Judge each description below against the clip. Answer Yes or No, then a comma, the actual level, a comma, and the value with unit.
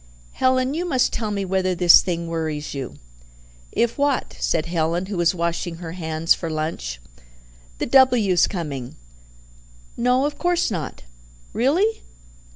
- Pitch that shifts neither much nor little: No, wide, 7.5 semitones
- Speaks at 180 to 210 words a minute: No, average, 140 wpm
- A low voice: No, medium, 180 Hz